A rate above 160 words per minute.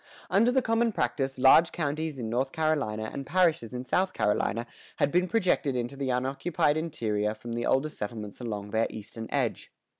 Yes: average, 180 wpm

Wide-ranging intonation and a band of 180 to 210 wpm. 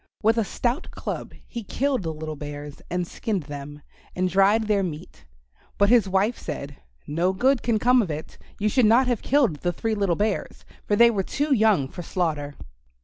Yes: wide, 6.3 semitones; average, 195 wpm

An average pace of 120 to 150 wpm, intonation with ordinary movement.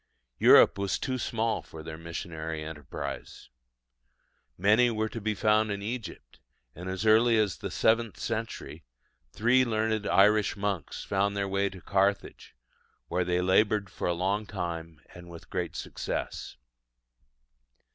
Yes: average, 140 wpm; average, 3.7 semitones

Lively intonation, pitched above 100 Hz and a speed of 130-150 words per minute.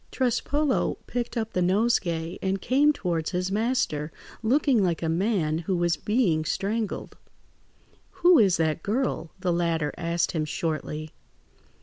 Yes: wide, 6.0 semitones; medium, 185 Hz; slow, 135 wpm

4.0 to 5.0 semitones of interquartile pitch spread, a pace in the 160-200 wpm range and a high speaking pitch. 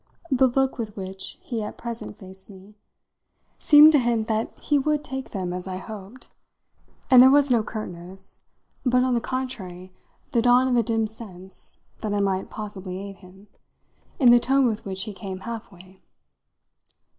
Yes: average, 4.7 semitones; average, 175 wpm; high, 220 Hz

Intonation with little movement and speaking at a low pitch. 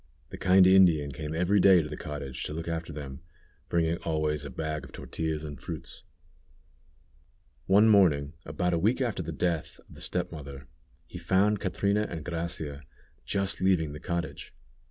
No: average, 3.8 semitones; very low, 80 Hz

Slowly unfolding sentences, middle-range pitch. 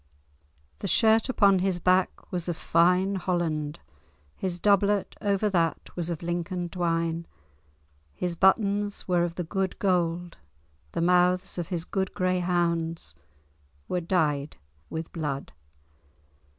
Yes: slow, 125 wpm; medium, 175 Hz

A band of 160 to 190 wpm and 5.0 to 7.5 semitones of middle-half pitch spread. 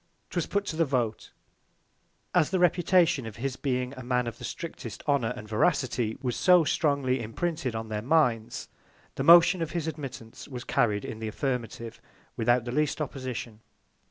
Yes: average, 170 wpm; average, 5.3 semitones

